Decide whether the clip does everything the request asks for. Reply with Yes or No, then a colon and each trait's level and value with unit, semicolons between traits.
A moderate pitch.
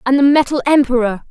No: very high, 265 Hz